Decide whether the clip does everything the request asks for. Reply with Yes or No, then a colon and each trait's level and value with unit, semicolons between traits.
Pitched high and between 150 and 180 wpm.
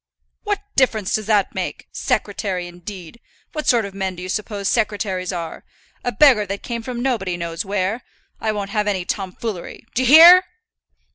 Yes: high, 205 Hz; average, 165 wpm